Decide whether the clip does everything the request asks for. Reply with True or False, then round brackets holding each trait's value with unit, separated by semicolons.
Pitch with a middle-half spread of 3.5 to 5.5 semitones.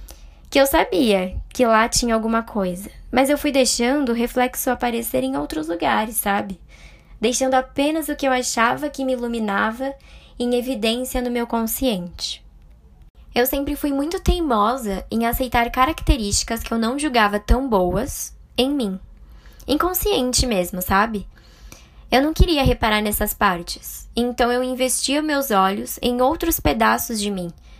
True (4.3 semitones)